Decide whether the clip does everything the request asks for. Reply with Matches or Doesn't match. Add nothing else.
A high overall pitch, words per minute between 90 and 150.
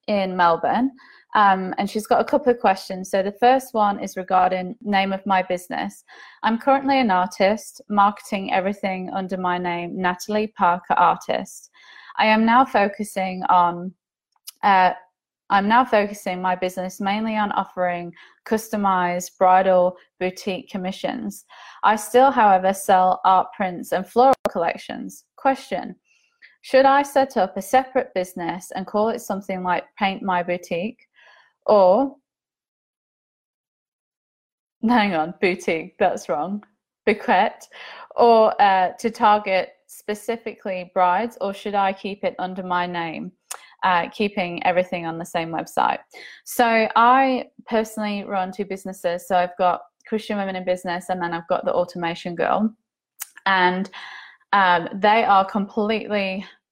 Matches